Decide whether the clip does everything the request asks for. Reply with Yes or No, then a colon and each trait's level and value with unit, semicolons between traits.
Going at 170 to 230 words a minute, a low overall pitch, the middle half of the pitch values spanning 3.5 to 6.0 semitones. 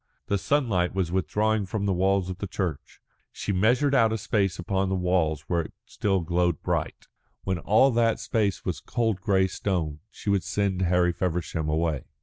No: average, 180 wpm; very low, 95 Hz; average, 2.8 semitones